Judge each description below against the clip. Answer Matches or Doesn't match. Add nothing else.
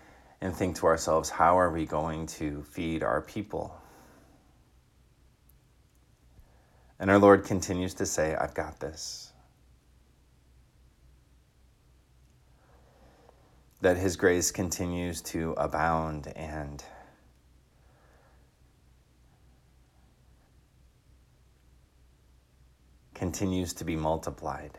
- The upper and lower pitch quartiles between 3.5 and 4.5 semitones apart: Doesn't match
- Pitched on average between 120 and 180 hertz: Doesn't match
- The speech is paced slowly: Matches